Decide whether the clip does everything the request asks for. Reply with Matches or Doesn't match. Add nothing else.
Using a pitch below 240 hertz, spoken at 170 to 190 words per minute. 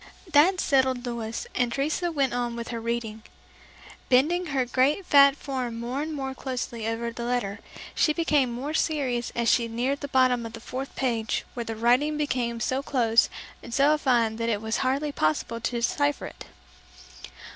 Doesn't match